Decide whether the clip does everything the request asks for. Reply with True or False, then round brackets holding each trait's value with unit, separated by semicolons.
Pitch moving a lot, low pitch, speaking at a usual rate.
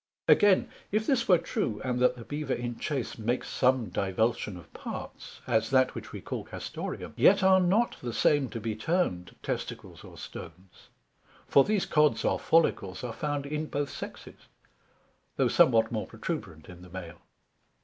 True (5.8 semitones; 125 Hz; 170 wpm)